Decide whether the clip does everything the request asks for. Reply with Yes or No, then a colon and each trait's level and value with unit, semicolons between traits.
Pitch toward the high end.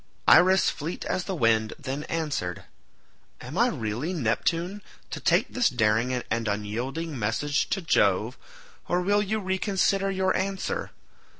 No: medium, 155 Hz